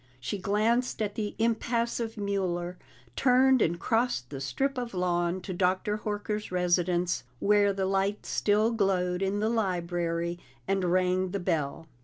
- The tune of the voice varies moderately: Yes, average, 3.4 semitones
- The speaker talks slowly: No, average, 145 wpm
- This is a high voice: Yes, high, 195 Hz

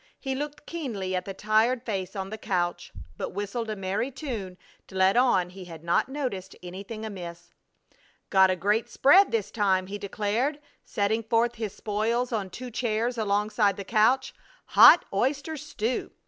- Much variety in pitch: No, average, 4.1 semitones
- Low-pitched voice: No, high, 215 Hz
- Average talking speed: Yes, average, 165 wpm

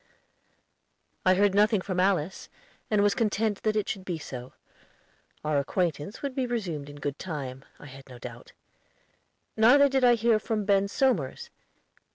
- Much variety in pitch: Yes, wide, 6.7 semitones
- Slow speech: No, average, 160 wpm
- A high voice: Yes, high, 195 Hz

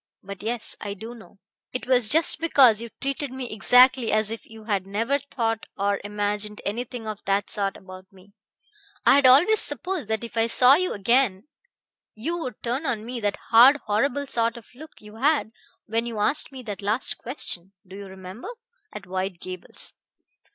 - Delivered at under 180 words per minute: No, average, 185 wpm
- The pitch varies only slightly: No, average, 4.0 semitones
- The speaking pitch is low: No, high, 225 Hz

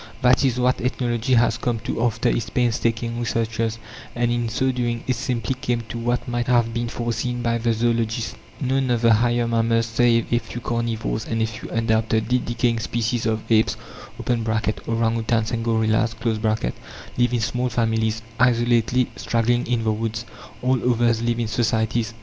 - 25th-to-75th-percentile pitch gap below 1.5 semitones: Yes, narrow, 1.1 semitones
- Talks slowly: No, average, 165 wpm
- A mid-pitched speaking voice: No, low, 115 Hz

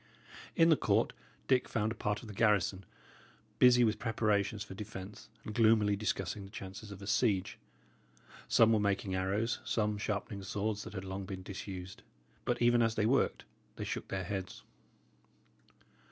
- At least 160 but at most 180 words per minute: Yes, average, 165 wpm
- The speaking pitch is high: No, low, 105 Hz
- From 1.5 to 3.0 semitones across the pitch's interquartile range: Yes, narrow, 2.4 semitones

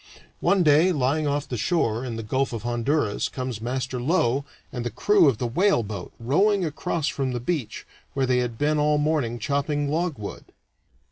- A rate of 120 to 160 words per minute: No, average, 180 wpm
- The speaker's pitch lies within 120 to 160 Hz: Yes, low, 135 Hz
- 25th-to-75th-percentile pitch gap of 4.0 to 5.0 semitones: Yes, average, 4.3 semitones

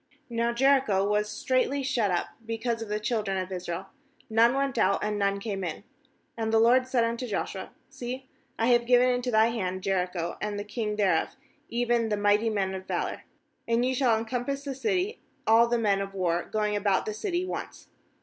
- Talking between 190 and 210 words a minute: Yes, average, 200 wpm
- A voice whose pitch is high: Yes, high, 225 Hz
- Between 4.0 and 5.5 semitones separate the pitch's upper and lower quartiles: No, average, 3.6 semitones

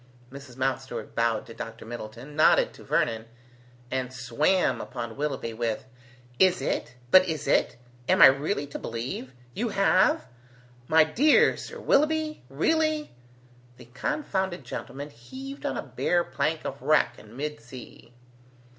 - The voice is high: No, medium, 140 Hz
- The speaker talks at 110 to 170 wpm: Yes, average, 140 wpm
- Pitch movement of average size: No, wide, 7.6 semitones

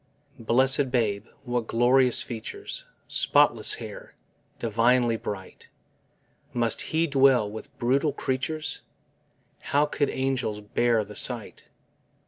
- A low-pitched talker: Yes, low, 125 Hz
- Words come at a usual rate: No, slow, 105 wpm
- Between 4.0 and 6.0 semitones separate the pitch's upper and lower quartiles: No, average, 3.3 semitones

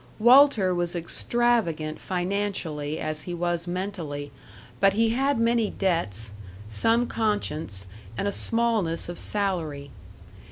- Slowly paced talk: Yes, slow, 115 wpm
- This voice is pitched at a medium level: Yes, medium, 180 Hz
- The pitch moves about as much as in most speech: No, wide, 6.2 semitones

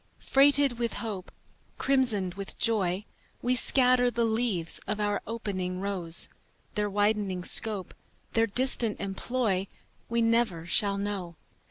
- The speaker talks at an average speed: No, slow, 125 wpm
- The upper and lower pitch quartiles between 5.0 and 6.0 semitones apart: No, average, 3.6 semitones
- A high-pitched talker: Yes, high, 210 Hz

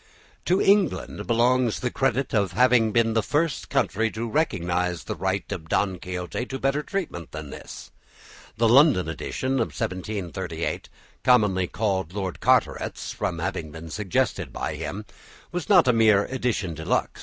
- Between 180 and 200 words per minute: No, average, 155 wpm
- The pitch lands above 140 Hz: No, low, 110 Hz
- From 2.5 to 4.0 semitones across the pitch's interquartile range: No, wide, 5.6 semitones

